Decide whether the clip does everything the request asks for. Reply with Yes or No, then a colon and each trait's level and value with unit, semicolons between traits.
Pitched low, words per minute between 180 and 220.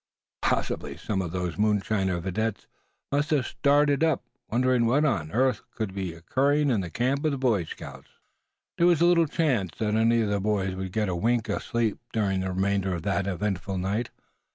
Yes: low, 105 Hz; average, 190 wpm